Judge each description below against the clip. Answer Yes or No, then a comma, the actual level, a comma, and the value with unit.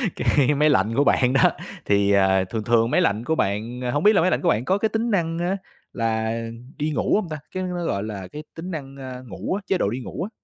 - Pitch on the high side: No, low, 135 Hz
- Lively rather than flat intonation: Yes, wide, 7.7 semitones